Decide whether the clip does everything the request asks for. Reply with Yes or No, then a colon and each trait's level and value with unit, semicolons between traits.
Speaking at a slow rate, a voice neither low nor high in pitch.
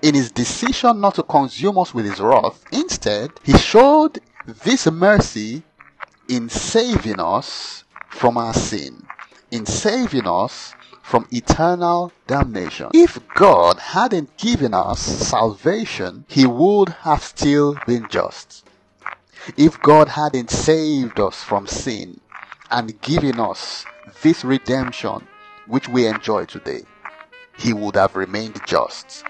Yes: slow, 125 wpm; medium, 155 Hz